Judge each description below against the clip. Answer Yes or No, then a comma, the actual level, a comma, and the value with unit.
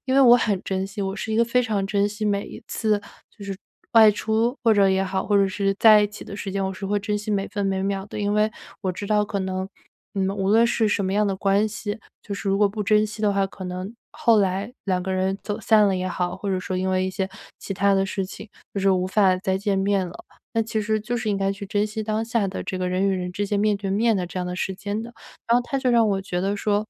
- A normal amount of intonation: No, narrow, 1.8 semitones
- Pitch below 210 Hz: Yes, high, 200 Hz